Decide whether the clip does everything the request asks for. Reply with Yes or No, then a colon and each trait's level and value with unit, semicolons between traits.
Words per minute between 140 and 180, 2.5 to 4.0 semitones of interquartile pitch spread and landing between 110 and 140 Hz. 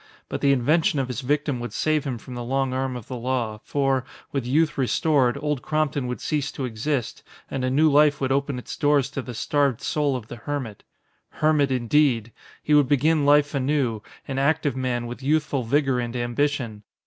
No: average, 195 wpm; average, 2.8 semitones; low, 135 Hz